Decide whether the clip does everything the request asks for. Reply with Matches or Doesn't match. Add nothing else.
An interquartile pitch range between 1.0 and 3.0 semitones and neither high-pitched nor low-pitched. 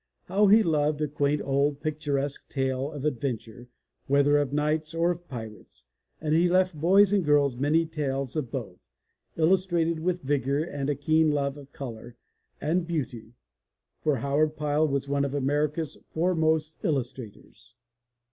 Matches